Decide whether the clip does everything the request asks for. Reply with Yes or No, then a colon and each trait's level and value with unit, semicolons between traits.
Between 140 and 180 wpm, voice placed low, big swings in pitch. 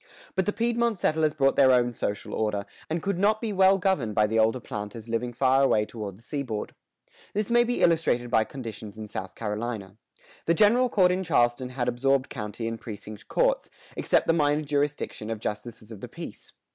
No: average, 195 wpm; low, 125 Hz; wide, 7.6 semitones